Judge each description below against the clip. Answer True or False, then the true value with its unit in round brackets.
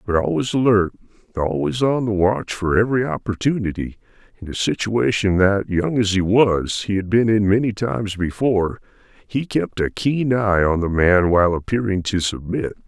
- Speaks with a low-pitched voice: True (105 Hz)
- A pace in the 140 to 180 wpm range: True (170 wpm)